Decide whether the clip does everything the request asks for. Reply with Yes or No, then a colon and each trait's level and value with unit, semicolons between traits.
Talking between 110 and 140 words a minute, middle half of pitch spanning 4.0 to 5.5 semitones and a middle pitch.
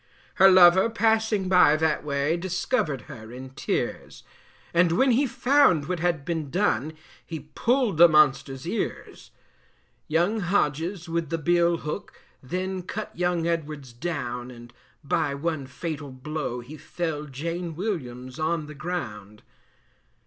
Yes: slow, 135 wpm; average, 4.3 semitones; medium, 165 Hz